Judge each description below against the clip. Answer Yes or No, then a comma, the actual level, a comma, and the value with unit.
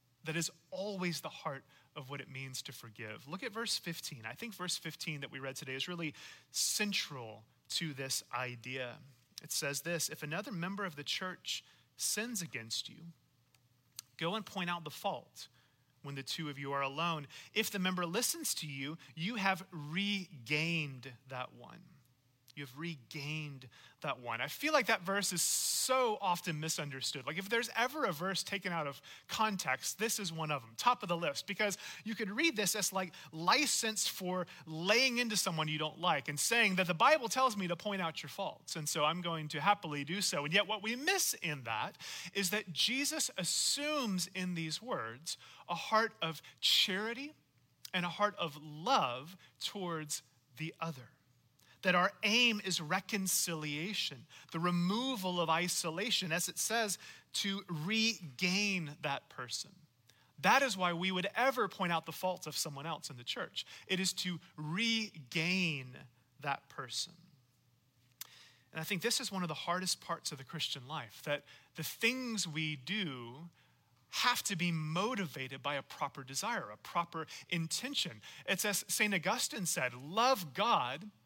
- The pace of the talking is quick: No, average, 170 wpm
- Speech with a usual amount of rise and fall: No, wide, 5.7 semitones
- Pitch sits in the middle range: Yes, medium, 170 Hz